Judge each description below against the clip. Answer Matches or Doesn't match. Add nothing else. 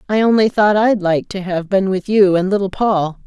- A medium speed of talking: Doesn't match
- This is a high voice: Matches